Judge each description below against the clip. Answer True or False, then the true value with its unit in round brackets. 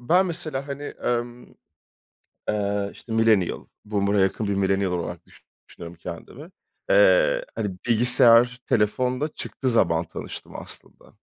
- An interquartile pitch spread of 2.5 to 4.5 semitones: False (5.6 semitones)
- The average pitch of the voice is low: True (115 Hz)